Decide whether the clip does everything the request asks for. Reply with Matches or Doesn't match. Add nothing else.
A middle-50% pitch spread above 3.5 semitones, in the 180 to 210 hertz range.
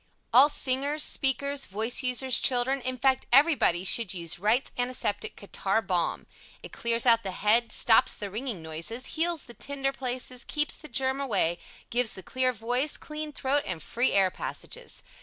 Doesn't match